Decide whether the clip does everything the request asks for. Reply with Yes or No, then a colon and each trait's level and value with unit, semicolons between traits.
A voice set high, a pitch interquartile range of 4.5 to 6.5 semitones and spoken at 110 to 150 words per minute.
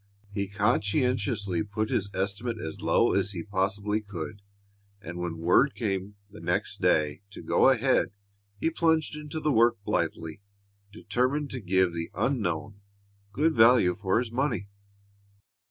No: low, 105 Hz; average, 4.8 semitones; average, 140 wpm